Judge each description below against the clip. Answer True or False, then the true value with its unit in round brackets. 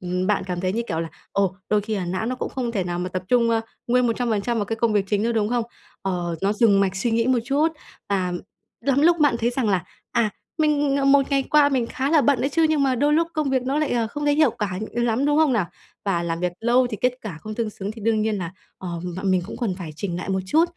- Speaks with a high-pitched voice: True (225 Hz)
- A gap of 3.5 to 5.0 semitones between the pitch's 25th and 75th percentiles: False (5.5 semitones)